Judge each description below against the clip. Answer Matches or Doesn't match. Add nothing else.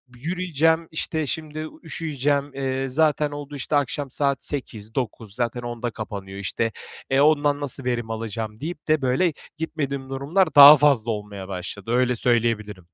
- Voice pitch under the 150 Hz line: Matches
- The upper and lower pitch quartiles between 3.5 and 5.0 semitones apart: Matches